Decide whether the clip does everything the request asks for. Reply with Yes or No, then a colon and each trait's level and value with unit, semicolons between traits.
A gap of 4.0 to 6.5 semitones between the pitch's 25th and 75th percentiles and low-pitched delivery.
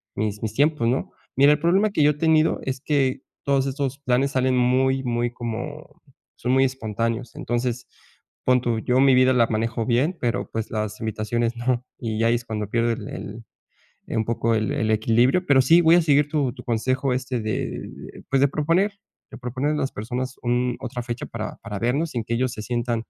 No: average, 2.8 semitones; low, 125 Hz